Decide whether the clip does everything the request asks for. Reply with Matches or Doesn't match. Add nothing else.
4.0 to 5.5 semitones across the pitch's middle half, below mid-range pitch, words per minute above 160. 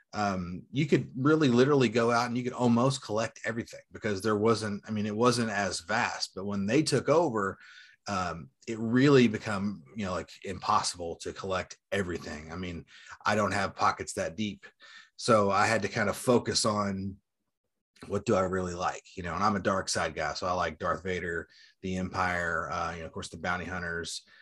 Matches